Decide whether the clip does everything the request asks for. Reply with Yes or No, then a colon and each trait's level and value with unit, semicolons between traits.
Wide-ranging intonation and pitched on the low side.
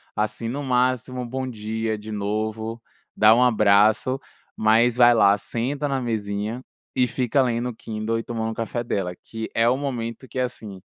No: narrow, 2.5 semitones; low, 115 Hz